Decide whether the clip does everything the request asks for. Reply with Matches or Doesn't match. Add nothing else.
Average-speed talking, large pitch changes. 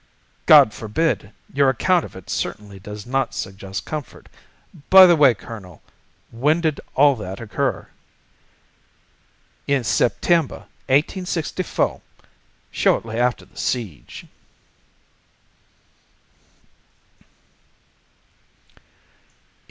Doesn't match